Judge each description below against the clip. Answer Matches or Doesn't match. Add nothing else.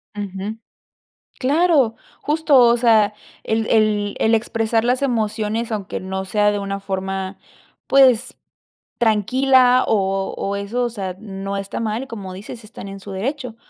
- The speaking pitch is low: Doesn't match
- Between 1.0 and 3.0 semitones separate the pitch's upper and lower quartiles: Doesn't match